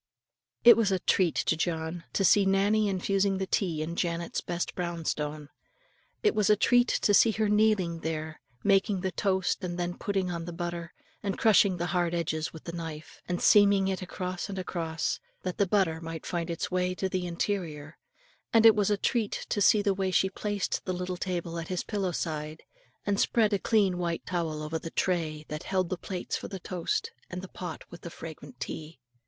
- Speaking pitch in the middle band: Yes, medium, 180 Hz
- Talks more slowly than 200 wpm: No, fast, 205 wpm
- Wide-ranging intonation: No, average, 2.9 semitones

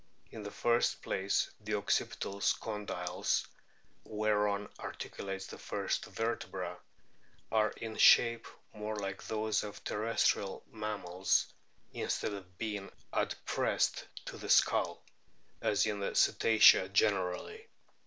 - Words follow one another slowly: Yes, slow, 115 wpm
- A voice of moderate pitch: No, low, 105 Hz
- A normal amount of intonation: No, narrow, 1.9 semitones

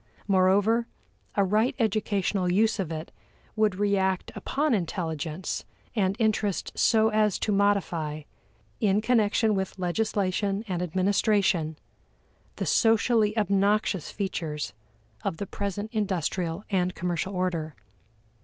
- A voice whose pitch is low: No, high, 200 Hz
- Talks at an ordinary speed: No, slow, 110 wpm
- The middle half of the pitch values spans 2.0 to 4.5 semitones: Yes, average, 3.0 semitones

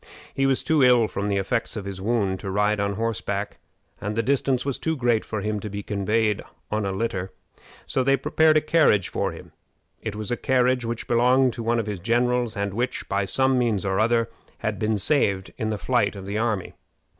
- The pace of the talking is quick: Yes, fast, 215 wpm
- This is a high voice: No, low, 110 Hz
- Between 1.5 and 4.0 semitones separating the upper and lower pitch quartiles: Yes, average, 3.5 semitones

